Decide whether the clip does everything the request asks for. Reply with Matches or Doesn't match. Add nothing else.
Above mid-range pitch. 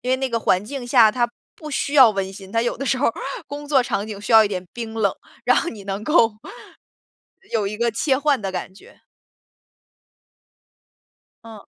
Matches